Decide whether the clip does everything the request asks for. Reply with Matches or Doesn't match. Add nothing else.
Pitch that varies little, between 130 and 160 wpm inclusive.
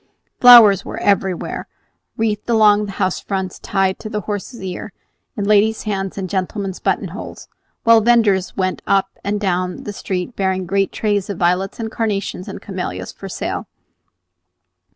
Matches